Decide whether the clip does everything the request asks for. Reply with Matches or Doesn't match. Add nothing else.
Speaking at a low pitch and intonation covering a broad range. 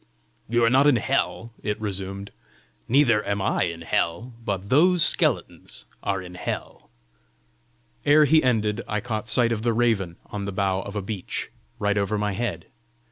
Doesn't match